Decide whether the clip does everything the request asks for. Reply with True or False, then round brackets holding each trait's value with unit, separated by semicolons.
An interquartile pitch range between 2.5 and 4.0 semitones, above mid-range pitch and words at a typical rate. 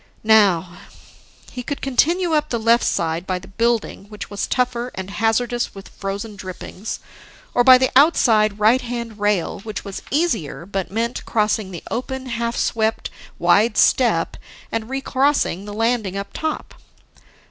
True (3.7 semitones; 225 Hz; 150 wpm)